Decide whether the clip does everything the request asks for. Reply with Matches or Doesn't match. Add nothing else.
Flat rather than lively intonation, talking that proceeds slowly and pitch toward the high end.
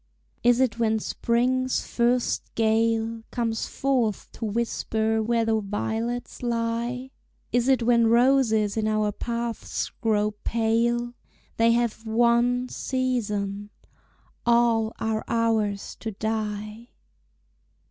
Matches